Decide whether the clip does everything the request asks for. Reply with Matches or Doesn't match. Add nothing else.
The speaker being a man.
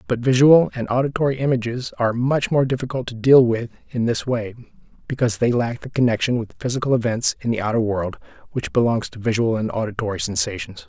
Matches